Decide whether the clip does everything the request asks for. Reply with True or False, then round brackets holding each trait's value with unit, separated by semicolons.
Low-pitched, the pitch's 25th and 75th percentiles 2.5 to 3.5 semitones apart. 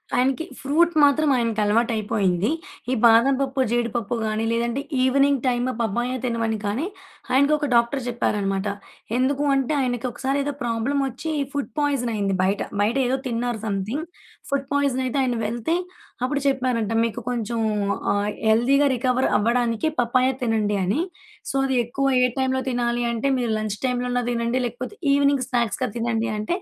False (245 Hz; 2.9 semitones)